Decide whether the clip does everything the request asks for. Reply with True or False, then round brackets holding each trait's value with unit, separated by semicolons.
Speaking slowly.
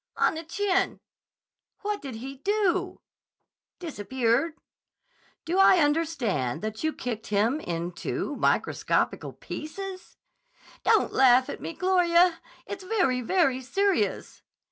True (110 wpm)